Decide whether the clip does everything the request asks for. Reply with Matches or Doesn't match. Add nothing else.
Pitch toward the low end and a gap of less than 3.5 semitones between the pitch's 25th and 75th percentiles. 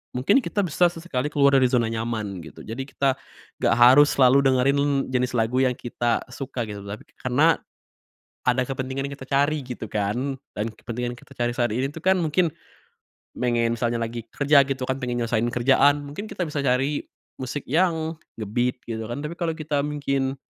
Matches